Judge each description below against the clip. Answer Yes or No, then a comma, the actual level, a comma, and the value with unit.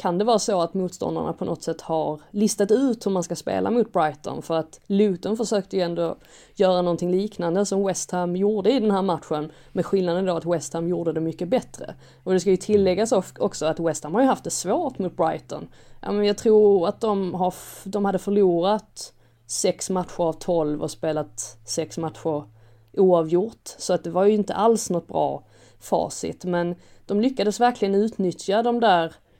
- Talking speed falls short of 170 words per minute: No, average, 190 wpm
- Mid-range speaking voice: Yes, medium, 180 Hz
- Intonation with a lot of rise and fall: No, average, 3.8 semitones